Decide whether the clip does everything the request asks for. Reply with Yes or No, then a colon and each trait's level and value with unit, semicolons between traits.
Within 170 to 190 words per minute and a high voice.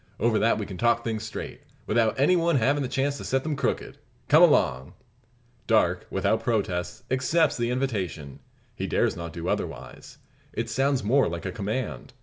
No: average, 175 wpm; low, 115 Hz